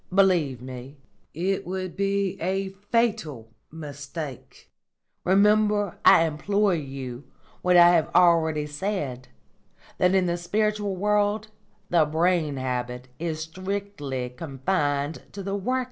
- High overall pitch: No, medium, 175 Hz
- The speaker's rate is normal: No, slow, 120 wpm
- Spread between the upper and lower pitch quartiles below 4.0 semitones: No, wide, 5.5 semitones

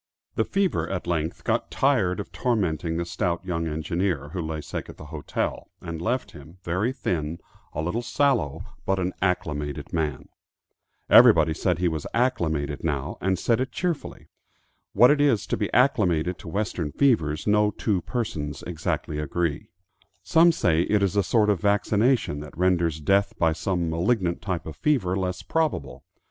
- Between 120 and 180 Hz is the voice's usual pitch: No, very low, 90 Hz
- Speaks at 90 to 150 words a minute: No, average, 165 wpm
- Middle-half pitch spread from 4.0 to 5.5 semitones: Yes, average, 4.9 semitones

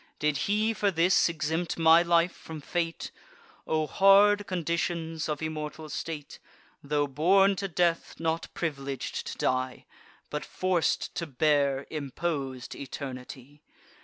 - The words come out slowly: Yes, slow, 125 wpm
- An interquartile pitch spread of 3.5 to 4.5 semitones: No, average, 3.1 semitones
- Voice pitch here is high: No, medium, 160 Hz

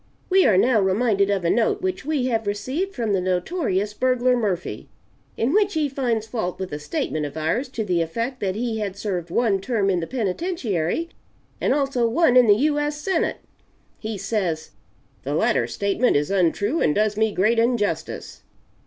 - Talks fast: No, average, 185 wpm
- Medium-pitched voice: No, high, 220 Hz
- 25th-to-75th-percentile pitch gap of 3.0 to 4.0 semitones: No, average, 5.0 semitones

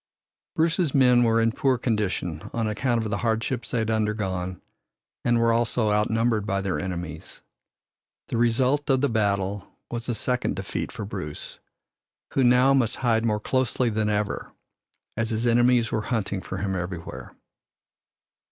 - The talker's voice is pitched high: No, low, 115 Hz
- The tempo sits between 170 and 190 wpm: No, average, 155 wpm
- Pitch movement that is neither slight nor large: Yes, average, 3.1 semitones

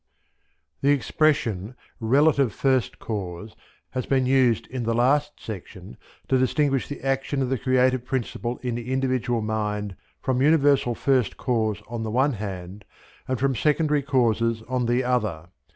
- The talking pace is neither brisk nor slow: Yes, average, 150 wpm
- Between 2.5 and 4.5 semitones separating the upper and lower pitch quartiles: Yes, average, 3.3 semitones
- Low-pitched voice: Yes, low, 125 Hz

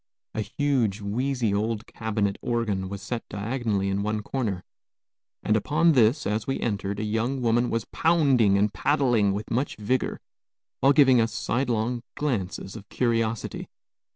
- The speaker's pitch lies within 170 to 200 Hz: No, low, 115 Hz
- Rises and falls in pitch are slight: No, average, 3.6 semitones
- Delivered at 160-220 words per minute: No, average, 150 wpm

